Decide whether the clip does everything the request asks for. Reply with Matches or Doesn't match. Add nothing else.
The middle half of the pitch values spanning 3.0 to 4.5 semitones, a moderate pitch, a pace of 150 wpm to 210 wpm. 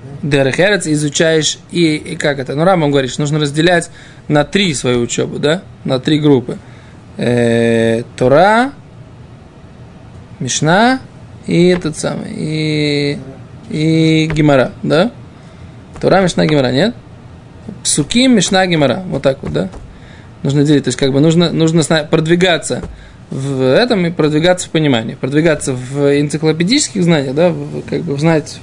Doesn't match